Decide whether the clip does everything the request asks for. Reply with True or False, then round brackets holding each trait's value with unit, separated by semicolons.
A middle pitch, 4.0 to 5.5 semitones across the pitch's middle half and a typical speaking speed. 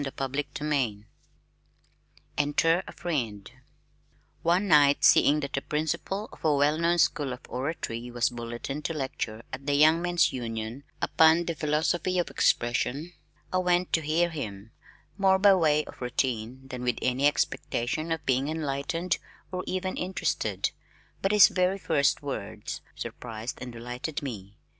True (145 Hz; 5.2 semitones; 150 wpm)